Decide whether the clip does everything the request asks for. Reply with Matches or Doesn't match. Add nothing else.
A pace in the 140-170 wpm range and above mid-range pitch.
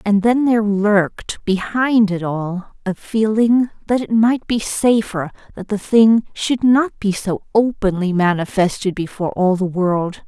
Matches